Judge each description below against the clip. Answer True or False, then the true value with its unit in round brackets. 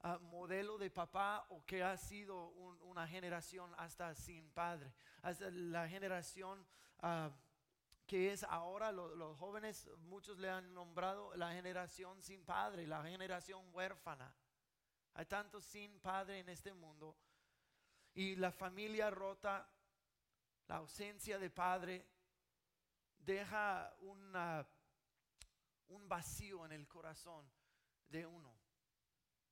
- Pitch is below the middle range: False (180 Hz)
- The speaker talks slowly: True (120 wpm)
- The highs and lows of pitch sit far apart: False (2.6 semitones)